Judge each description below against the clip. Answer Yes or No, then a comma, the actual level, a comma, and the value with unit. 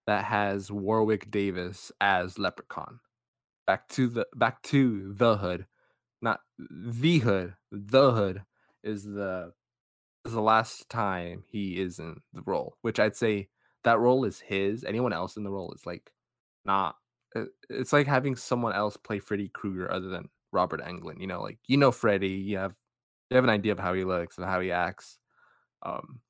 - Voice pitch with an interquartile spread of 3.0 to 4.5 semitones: Yes, average, 3.5 semitones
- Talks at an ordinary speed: Yes, average, 180 wpm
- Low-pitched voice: Yes, low, 100 Hz